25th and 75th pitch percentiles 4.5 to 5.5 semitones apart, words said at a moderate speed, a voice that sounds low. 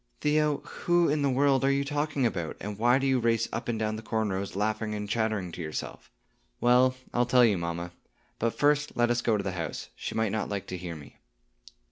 No: average, 5.0 semitones; fast, 225 wpm; low, 115 Hz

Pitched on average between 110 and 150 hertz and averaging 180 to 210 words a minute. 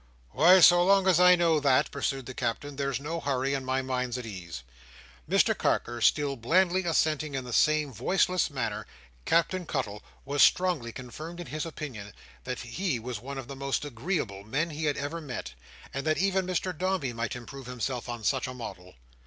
Yes: medium, 140 Hz; average, 190 wpm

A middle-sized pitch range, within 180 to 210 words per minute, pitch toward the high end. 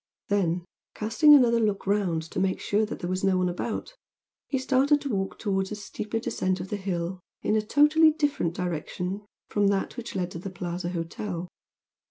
Yes: average, 3.9 semitones; average, 190 wpm; high, 200 Hz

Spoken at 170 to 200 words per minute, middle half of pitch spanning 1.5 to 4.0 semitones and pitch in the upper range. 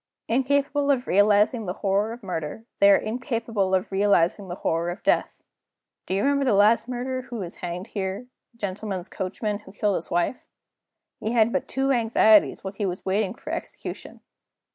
Yes: average, 180 wpm; average, 3.7 semitones; high, 210 Hz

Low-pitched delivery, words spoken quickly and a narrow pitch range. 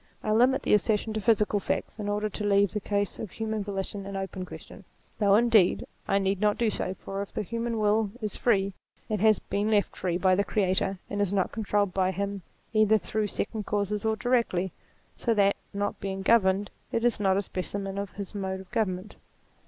No: high, 205 Hz; fast, 210 wpm; narrow, 1.9 semitones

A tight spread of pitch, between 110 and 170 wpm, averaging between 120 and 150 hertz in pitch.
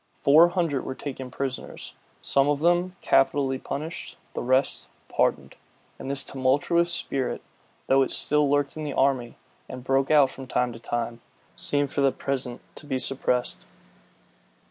Yes: narrow, 2.1 semitones; average, 155 wpm; low, 135 Hz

